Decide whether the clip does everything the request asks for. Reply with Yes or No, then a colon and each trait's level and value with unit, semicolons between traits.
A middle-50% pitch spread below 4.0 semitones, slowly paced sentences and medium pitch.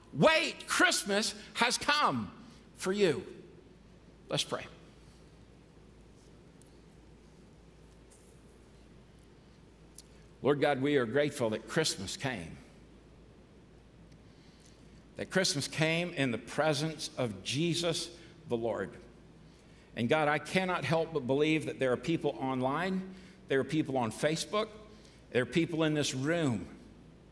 No: average, 5.1 semitones; slow, 110 wpm; medium, 155 Hz